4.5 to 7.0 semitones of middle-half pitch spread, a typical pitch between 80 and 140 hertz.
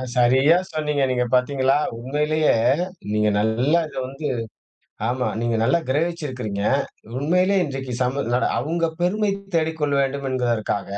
No: average, 3.9 semitones; low, 135 Hz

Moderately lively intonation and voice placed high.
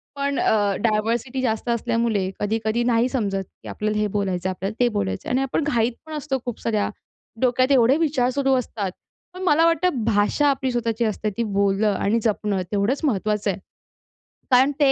Yes: average, 4.1 semitones; high, 230 Hz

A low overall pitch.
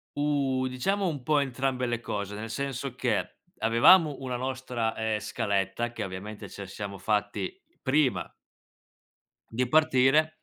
Yes: low, 125 Hz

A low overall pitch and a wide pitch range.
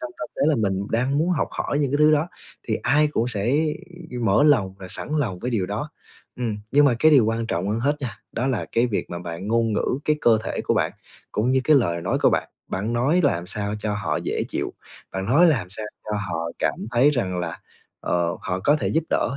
Yes: low, 115 Hz; wide, 6.3 semitones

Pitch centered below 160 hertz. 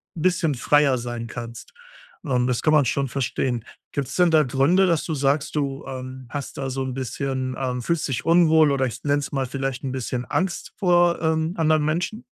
Yes: medium, 140 Hz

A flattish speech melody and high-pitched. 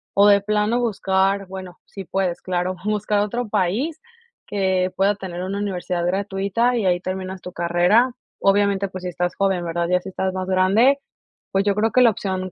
Yes: narrow, 2.0 semitones; high, 195 Hz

